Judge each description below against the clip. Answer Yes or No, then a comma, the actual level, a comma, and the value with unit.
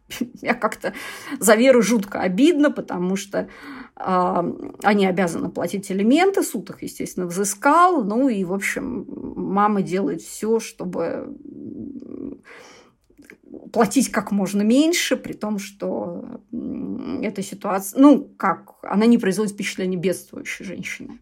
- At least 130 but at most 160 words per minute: No, average, 120 wpm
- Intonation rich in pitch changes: Yes, wide, 5.8 semitones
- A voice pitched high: Yes, high, 235 Hz